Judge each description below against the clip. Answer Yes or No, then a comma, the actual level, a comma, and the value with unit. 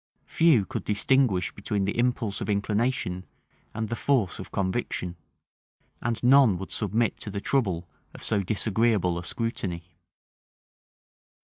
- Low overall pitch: Yes, low, 105 Hz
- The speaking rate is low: Yes, slow, 130 wpm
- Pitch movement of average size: Yes, average, 3.8 semitones